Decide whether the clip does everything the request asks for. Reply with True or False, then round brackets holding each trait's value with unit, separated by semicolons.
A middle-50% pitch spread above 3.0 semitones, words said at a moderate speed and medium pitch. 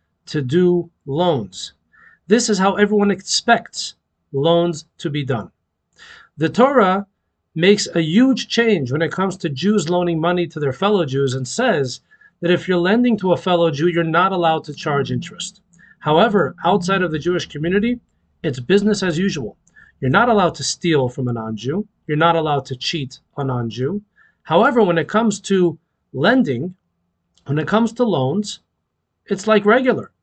True (5.5 semitones; 170 wpm; 175 Hz)